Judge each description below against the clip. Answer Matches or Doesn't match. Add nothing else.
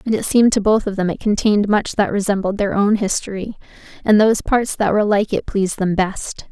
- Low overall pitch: Doesn't match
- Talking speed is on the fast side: Matches